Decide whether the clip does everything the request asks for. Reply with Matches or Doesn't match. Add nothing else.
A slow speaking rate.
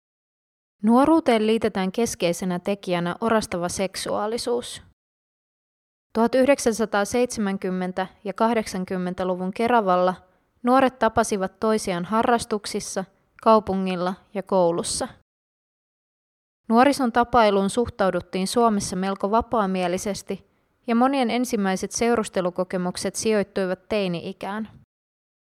Matches